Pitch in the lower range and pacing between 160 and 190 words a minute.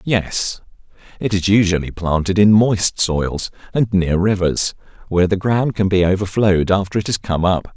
Yes: very low, 95 Hz; average, 170 wpm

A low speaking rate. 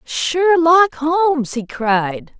Yes: slow, 100 wpm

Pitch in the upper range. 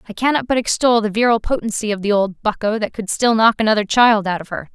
Yes: high, 220 Hz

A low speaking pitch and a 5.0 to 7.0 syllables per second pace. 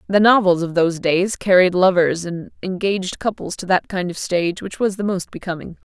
No: medium, 185 Hz; 5.4 syllables/s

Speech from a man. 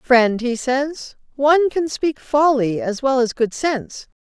No: female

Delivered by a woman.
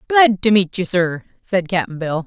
Yes: female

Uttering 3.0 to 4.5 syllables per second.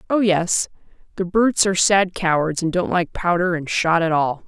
No: 5.0 syllables/s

